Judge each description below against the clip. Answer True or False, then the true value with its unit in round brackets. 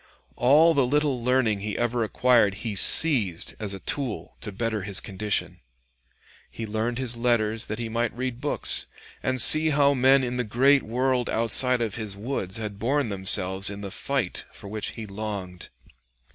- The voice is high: False (115 Hz)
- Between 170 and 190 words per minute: True (175 wpm)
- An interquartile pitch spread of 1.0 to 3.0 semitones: False (3.6 semitones)